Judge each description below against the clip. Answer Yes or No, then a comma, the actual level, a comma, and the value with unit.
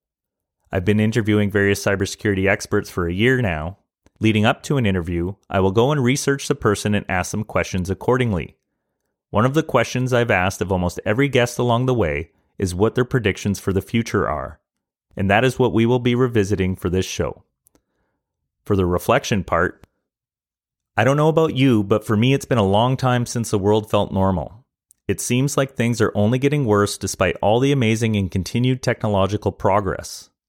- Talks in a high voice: No, low, 105 Hz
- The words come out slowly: No, average, 190 wpm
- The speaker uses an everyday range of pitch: Yes, average, 4.2 semitones